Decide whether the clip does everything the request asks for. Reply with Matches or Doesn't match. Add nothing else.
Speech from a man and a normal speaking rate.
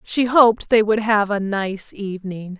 Doesn't match